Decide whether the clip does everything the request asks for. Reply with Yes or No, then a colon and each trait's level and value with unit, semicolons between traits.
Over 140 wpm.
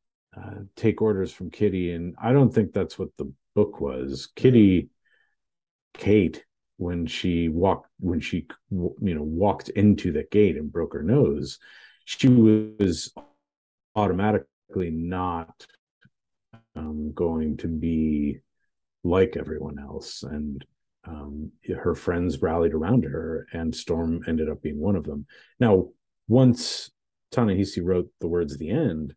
No: slow, 135 wpm